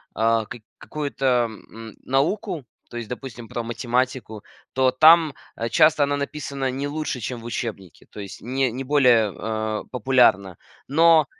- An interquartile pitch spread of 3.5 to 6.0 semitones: Yes, average, 3.9 semitones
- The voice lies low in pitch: Yes, low, 125 Hz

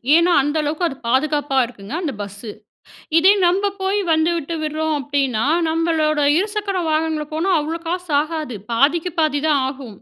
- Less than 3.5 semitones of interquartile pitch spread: Yes, average, 3.1 semitones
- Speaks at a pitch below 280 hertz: No, very high, 310 Hz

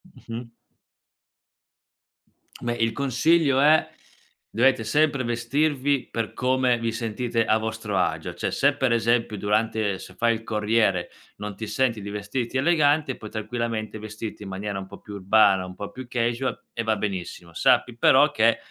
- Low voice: Yes, low, 115 Hz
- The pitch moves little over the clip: No, average, 3.3 semitones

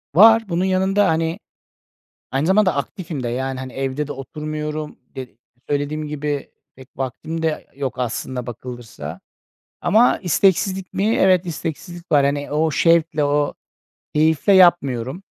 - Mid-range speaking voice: Yes, medium, 150 Hz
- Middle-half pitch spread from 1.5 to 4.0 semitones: No, average, 4.6 semitones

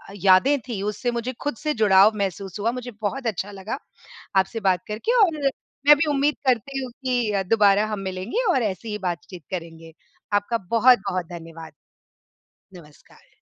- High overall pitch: Yes, high, 210 Hz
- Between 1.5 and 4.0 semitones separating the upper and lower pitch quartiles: No, average, 4.8 semitones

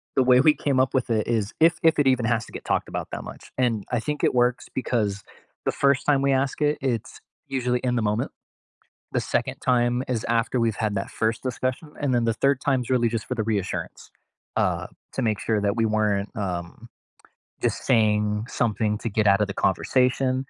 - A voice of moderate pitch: No, low, 120 Hz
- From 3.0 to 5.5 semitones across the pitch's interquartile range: Yes, average, 3.3 semitones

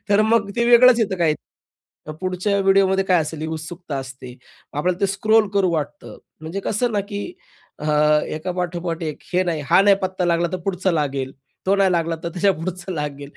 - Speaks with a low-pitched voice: No, medium, 180 Hz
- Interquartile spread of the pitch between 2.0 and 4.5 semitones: Yes, average, 3.7 semitones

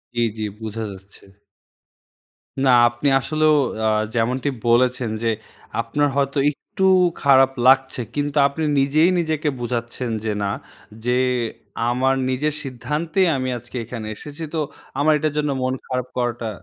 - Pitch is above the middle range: No, low, 130 Hz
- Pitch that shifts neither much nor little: Yes, average, 3.7 semitones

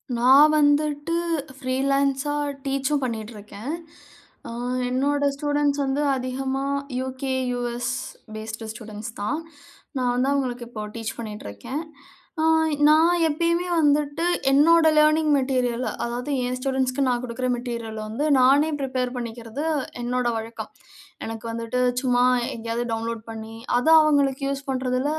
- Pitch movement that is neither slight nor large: Yes, average, 3.4 semitones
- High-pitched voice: Yes, very high, 255 Hz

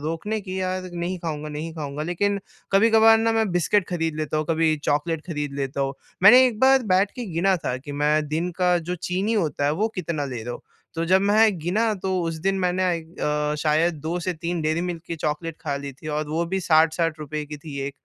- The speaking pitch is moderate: Yes, medium, 165 Hz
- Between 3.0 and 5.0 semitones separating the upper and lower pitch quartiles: Yes, average, 3.5 semitones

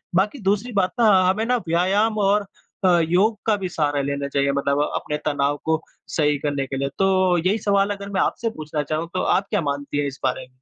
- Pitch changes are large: Yes, wide, 5.7 semitones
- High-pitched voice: No, medium, 170 Hz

